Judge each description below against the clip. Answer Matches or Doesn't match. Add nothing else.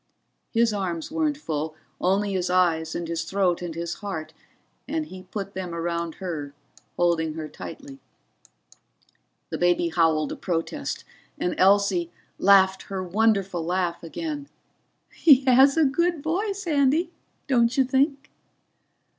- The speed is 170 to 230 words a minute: Doesn't match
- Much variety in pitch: Matches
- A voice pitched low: Doesn't match